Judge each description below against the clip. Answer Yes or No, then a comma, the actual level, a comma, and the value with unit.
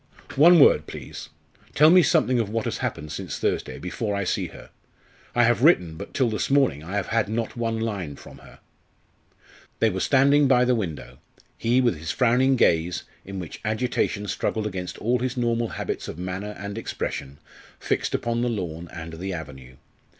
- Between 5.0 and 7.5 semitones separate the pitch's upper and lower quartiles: Yes, wide, 5.5 semitones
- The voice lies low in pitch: Yes, low, 110 Hz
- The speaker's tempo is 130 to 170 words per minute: No, average, 185 wpm